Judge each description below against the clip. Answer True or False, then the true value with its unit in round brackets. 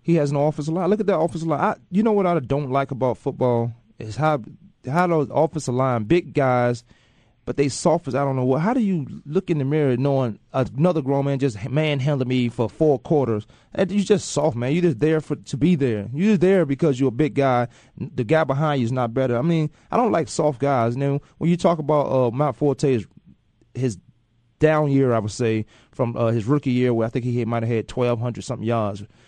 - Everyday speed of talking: False (250 wpm)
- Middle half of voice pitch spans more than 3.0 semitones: True (4.2 semitones)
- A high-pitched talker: False (140 Hz)